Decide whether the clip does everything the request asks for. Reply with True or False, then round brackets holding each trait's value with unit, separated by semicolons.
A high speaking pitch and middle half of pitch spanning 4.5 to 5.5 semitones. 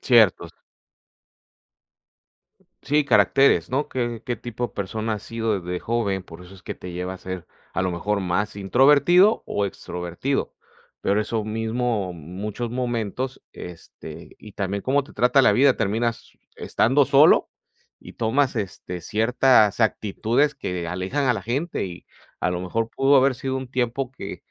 False (115 Hz; 5.2 semitones)